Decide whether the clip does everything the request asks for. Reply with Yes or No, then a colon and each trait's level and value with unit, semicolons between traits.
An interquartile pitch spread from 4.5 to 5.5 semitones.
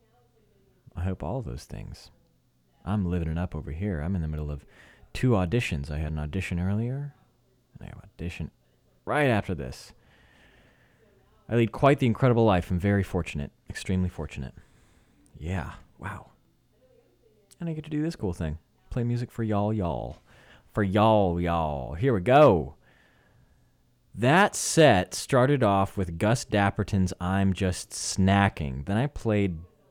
Yes: average, 5.2 semitones